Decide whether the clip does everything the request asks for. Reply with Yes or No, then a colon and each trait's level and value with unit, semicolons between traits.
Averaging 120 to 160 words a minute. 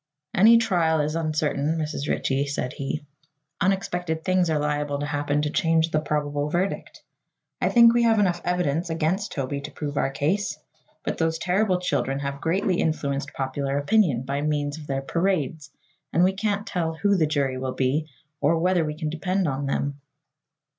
No: average, 175 wpm